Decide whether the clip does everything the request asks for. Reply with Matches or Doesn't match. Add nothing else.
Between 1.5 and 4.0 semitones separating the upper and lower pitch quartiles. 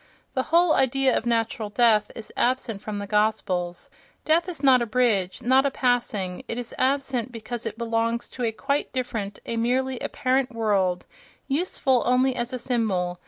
Matches